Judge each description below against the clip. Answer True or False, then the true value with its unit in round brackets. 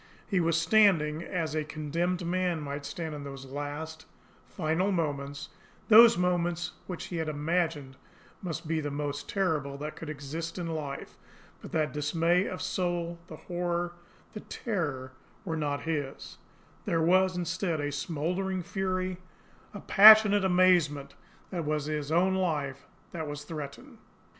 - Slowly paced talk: False (150 wpm)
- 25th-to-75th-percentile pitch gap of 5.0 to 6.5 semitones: False (3.4 semitones)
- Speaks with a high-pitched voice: False (165 Hz)